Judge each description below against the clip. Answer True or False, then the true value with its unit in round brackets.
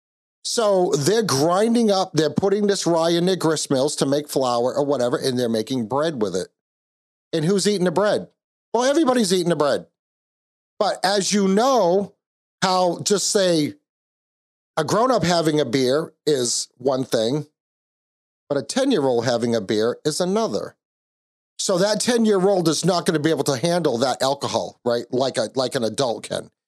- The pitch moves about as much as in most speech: False (6.6 semitones)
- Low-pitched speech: False (165 Hz)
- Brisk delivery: False (170 wpm)